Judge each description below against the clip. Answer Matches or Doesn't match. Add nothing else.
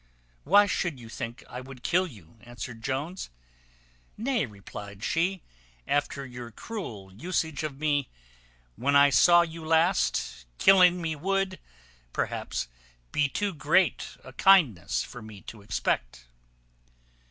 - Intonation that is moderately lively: Doesn't match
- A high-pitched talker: Doesn't match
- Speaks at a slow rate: Matches